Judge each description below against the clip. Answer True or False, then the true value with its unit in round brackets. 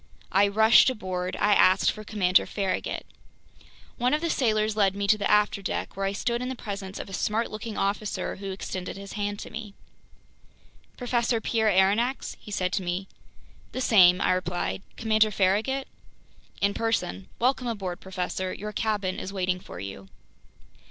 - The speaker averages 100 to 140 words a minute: False (165 wpm)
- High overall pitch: True (205 Hz)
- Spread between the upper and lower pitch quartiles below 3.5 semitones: True (2.7 semitones)